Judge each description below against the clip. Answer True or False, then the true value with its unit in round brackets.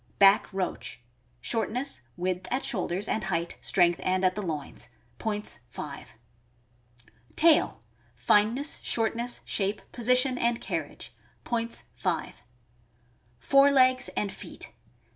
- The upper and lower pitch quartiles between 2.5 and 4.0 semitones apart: False (5.2 semitones)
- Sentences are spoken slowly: True (120 wpm)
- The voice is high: True (210 Hz)